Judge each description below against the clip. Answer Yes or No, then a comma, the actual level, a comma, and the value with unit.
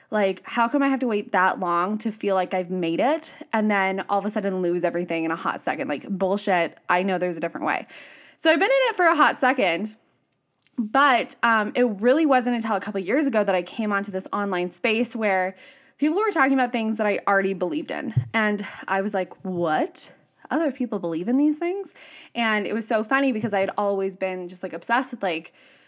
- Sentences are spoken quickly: Yes, fast, 230 wpm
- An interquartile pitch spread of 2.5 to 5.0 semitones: No, wide, 5.4 semitones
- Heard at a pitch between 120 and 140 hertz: No, high, 210 Hz